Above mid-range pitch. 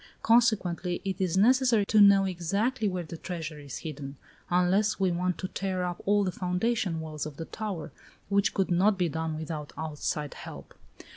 No: medium, 180 Hz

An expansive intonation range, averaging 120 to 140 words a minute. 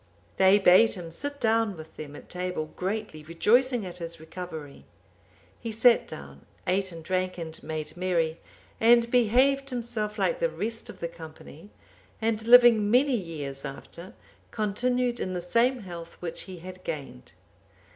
No: wide, 5.8 semitones; average, 155 wpm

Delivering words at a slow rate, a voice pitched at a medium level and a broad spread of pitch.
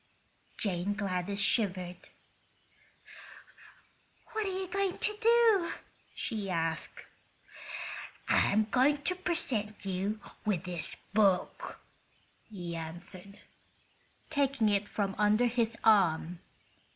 No: slow, 95 wpm; high, 210 Hz; wide, 7.1 semitones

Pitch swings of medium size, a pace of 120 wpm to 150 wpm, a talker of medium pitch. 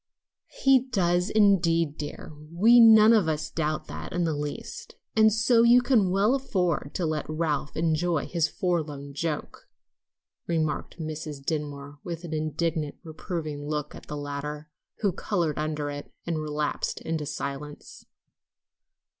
Yes: average, 3.5 semitones; average, 140 wpm; medium, 160 Hz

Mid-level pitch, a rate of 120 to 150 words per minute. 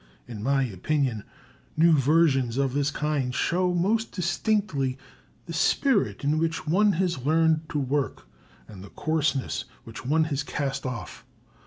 Yes: medium, 150 Hz; average, 145 wpm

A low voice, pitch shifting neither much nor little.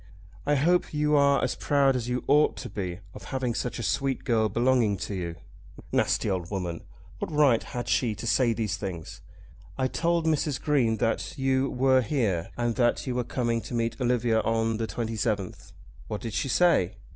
Yes: low, 120 Hz; average, 3.7 semitones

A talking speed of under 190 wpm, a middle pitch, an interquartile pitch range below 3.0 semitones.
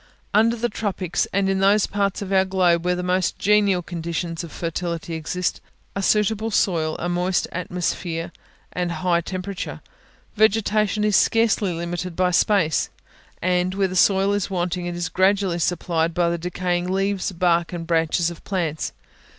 Yes: average, 165 wpm; medium, 180 Hz; narrow, 2.4 semitones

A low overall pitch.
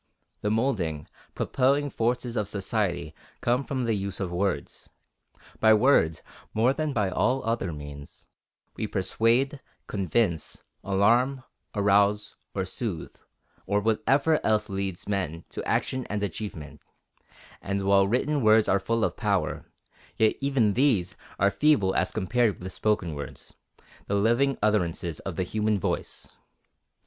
Yes: low, 105 Hz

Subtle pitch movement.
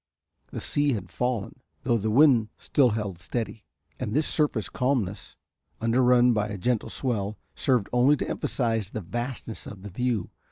No: average, 3.2 semitones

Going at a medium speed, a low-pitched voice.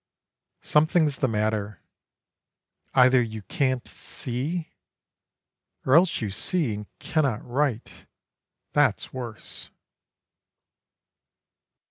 No: slow, 80 wpm; low, 130 Hz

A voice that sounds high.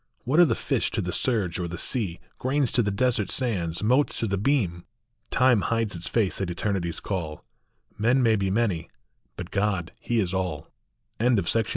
No: low, 105 Hz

